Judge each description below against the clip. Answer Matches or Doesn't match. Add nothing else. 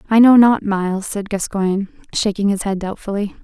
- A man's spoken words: Doesn't match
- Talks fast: Doesn't match